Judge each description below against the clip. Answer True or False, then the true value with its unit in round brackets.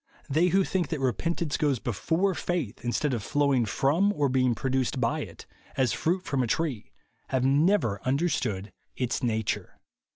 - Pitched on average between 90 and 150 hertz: True (135 Hz)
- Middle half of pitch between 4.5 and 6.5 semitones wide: True (5.3 semitones)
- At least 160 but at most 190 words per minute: True (165 wpm)